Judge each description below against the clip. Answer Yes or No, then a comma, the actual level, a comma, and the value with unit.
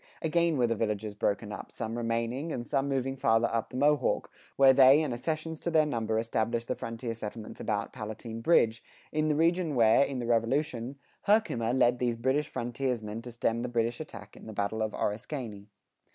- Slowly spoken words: No, average, 190 wpm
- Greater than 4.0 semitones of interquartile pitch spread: No, average, 3.6 semitones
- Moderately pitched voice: No, low, 120 Hz